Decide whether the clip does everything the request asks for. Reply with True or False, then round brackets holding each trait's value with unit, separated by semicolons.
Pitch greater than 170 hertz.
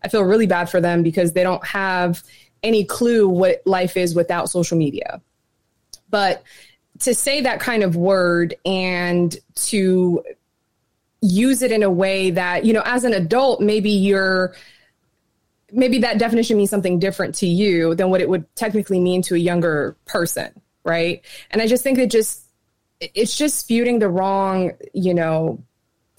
True (190 Hz)